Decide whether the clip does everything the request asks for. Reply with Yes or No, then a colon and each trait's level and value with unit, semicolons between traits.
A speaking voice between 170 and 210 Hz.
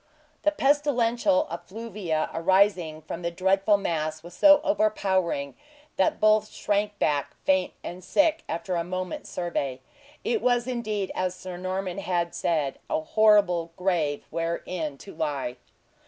Yes: medium, 185 Hz